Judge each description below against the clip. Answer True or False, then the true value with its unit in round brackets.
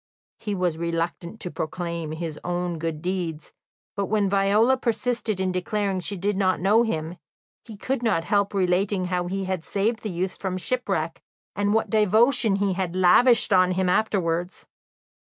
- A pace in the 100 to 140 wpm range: False (170 wpm)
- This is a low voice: False (190 Hz)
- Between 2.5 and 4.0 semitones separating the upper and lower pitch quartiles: True (2.9 semitones)